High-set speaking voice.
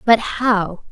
Yes: high, 215 Hz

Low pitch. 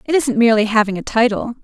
No: high, 230 Hz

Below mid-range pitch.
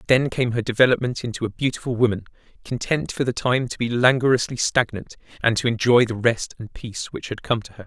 Yes: low, 120 Hz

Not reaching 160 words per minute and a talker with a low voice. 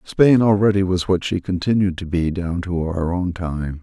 No: fast, 205 wpm; very low, 90 Hz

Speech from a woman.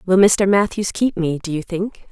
Yes: female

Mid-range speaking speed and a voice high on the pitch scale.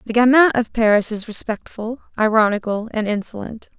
Yes: average, 145 wpm; high, 225 Hz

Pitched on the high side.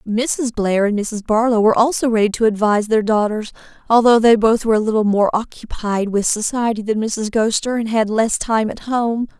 Yes: high, 220 Hz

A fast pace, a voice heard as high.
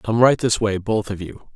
No: fast, 270 wpm; low, 110 Hz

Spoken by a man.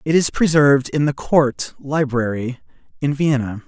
Yes: male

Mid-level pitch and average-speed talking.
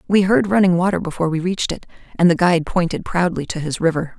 No: medium, 175 Hz; fast, 230 wpm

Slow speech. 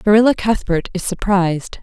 Yes: slow, 130 wpm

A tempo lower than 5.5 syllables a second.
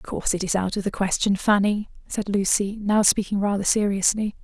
No: 5.6 syllables/s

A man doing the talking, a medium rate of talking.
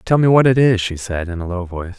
No: male; fast, 330 wpm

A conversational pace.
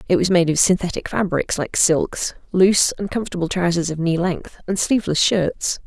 Yes: average, 185 wpm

